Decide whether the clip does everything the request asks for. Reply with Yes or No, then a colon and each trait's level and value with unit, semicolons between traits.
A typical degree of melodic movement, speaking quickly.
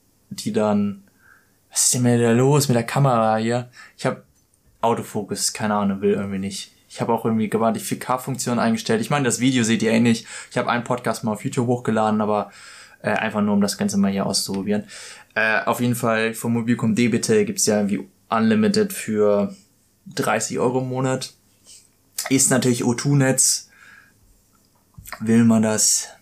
No: average, 3.5 semitones; average, 175 wpm